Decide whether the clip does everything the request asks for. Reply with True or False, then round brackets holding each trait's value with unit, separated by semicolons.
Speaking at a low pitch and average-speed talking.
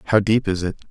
False (100 Hz; 265 wpm)